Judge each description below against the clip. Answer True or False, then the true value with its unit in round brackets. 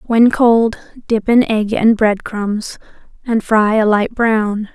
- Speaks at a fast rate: False (165 wpm)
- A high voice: True (220 Hz)